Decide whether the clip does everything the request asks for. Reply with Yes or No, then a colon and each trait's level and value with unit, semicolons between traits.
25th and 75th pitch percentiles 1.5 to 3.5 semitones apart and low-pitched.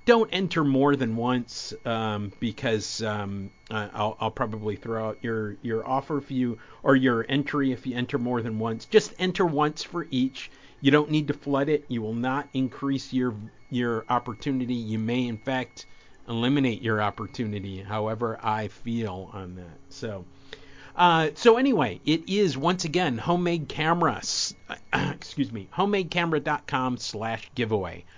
No: average, 4.7 semitones; low, 125 Hz